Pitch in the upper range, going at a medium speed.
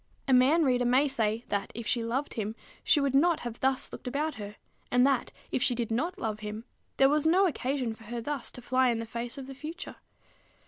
No: very high, 250 Hz; fast, 230 wpm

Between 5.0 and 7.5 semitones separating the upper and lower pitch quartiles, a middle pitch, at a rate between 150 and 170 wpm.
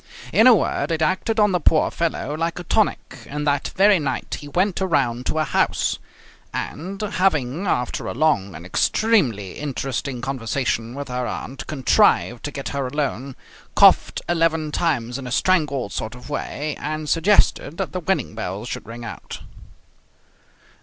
Yes: wide, 5.6 semitones; medium, 145 Hz; average, 165 wpm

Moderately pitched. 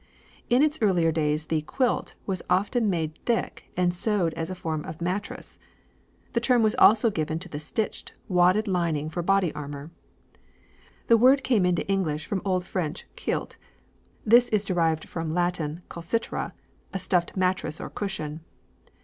Yes: medium, 180 Hz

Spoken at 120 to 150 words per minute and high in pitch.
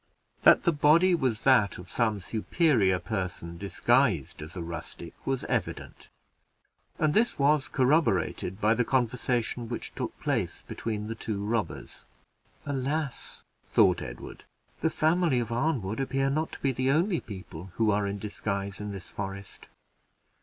No: average, 145 wpm; low, 115 Hz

